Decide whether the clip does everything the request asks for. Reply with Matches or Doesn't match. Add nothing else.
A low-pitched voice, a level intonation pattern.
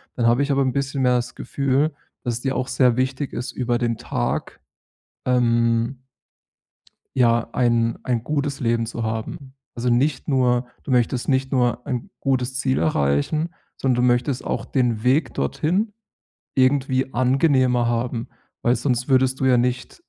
Matches